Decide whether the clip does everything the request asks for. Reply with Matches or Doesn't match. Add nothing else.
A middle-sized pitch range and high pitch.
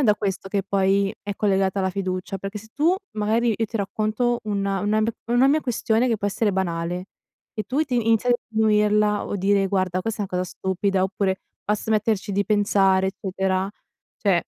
Doesn't match